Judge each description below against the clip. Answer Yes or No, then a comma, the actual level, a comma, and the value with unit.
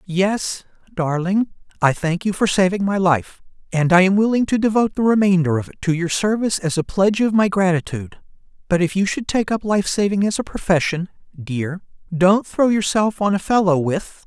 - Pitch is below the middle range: No, high, 190 Hz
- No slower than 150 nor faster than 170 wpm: No, average, 200 wpm